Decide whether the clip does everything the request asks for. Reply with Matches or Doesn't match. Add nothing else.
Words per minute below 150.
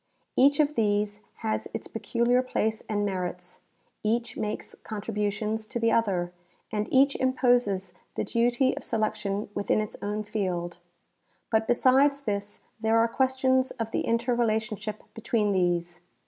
Matches